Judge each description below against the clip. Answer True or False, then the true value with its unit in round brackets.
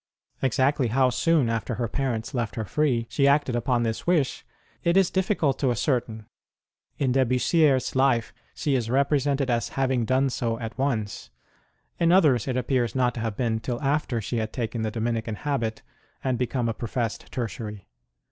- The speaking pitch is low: True (125 Hz)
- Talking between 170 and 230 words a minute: True (185 wpm)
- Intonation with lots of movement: False (3.1 semitones)